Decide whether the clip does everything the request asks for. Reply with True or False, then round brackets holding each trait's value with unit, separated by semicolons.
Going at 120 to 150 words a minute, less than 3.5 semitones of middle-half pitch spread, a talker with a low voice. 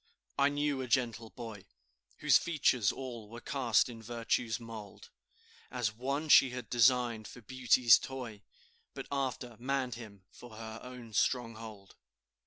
True (140 wpm; 2.5 semitones; 120 Hz)